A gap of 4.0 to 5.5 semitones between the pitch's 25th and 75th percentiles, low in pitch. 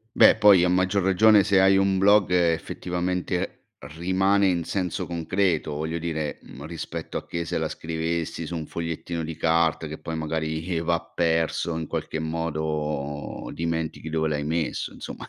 No: narrow, 2.4 semitones; very low, 85 Hz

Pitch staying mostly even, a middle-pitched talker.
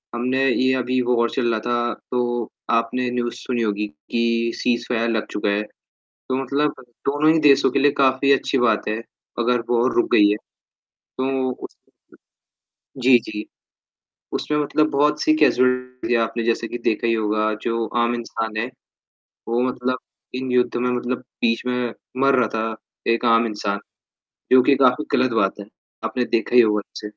No: narrow, 1.9 semitones; low, 120 Hz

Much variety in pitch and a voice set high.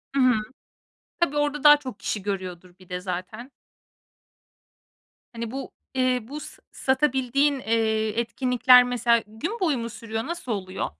No: average, 4.0 semitones; high, 245 Hz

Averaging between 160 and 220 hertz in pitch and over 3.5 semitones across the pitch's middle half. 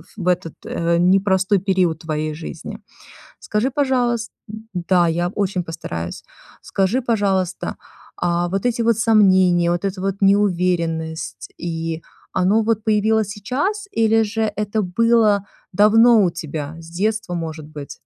Yes: high, 190 Hz; average, 4.3 semitones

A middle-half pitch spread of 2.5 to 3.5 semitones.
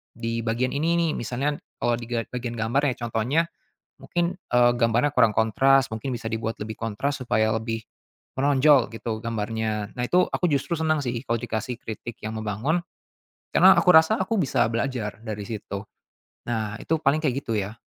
No: average, 4.1 semitones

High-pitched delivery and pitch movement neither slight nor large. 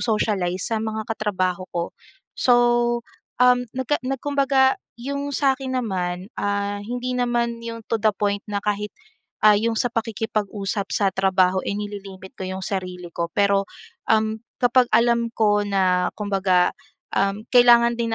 Yes: high, 210 Hz; average, 3.4 semitones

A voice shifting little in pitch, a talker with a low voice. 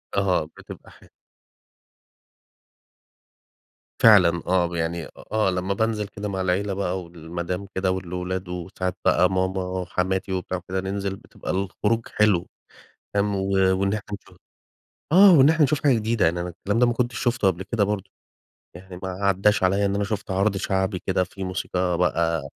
Yes: narrow, 2.1 semitones; very low, 95 Hz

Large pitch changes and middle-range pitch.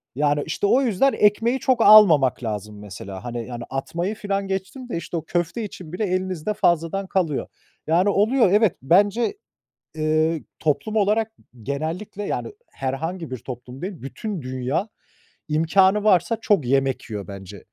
Yes: wide, 7.3 semitones; medium, 175 Hz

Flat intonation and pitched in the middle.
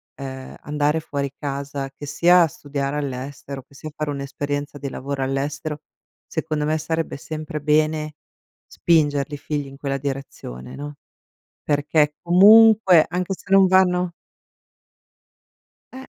Yes: narrow, 2.2 semitones; medium, 145 Hz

